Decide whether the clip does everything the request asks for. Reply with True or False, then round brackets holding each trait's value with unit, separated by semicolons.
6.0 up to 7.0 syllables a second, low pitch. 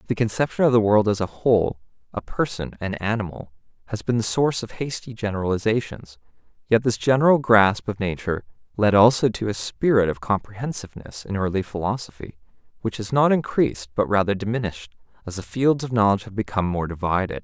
True (6.1 syllables/s; 105 Hz)